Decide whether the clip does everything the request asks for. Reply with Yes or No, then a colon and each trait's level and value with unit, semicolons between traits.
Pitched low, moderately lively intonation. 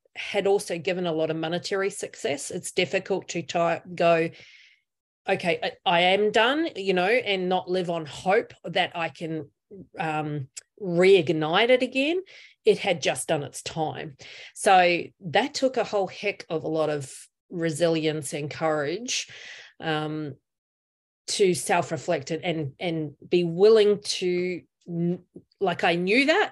No: medium, 175 Hz; average, 3.4 semitones